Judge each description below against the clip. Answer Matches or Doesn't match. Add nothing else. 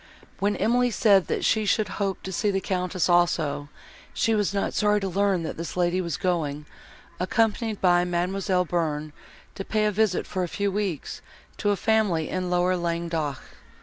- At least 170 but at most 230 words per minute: Matches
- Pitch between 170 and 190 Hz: Matches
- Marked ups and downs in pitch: Doesn't match